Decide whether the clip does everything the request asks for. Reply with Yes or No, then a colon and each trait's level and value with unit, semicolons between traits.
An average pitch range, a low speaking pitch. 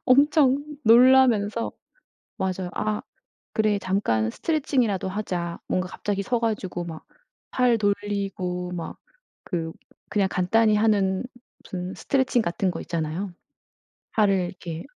No: average, 4.0 semitones; high, 200 Hz